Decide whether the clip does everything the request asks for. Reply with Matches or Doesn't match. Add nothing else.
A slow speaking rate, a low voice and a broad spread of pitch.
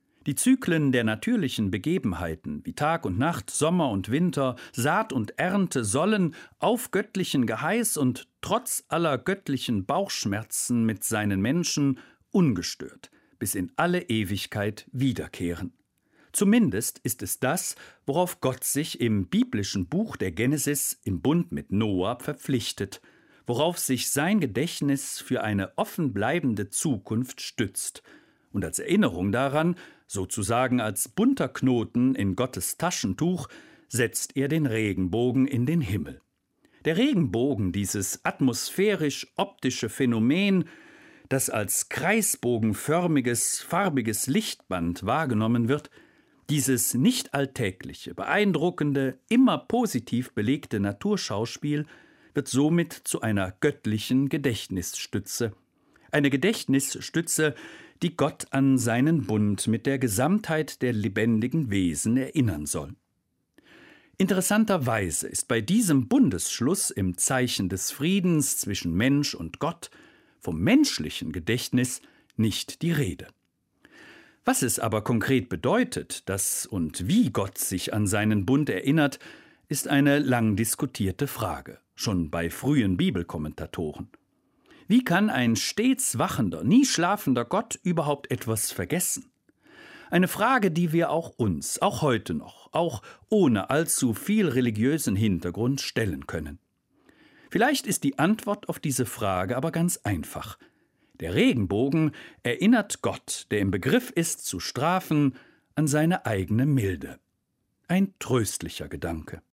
Matches